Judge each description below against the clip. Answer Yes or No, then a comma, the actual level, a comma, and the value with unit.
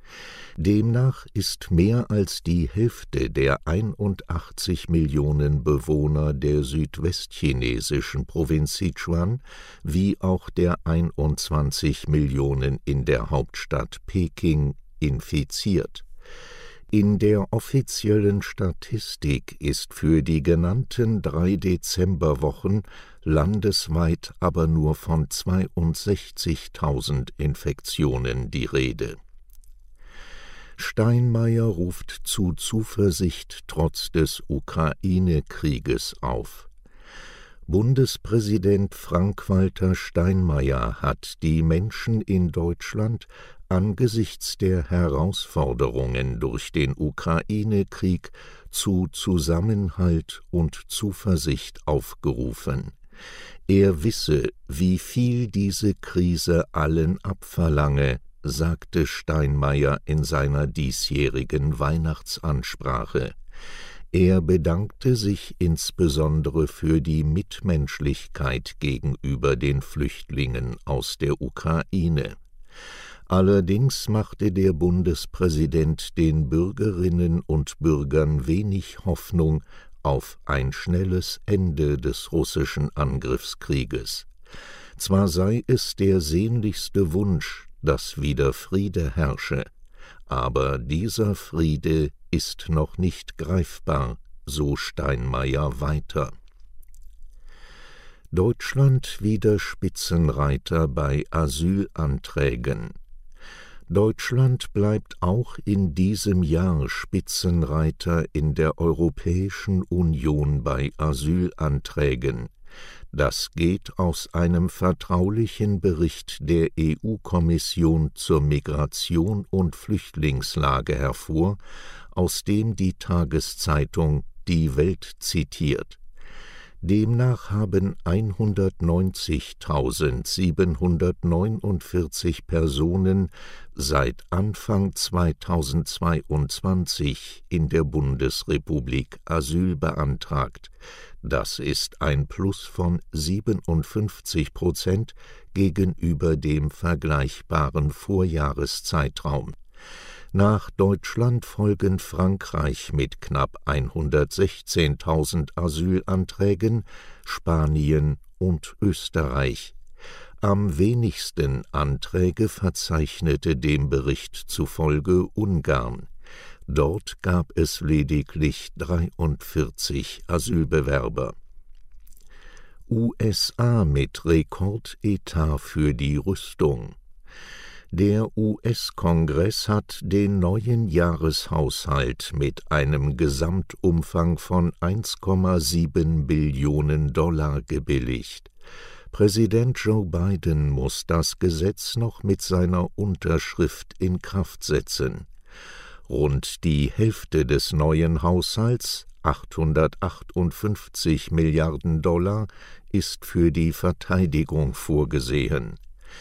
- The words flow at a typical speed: No, slow, 75 wpm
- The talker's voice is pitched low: Yes, very low, 85 Hz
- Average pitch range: Yes, average, 4.3 semitones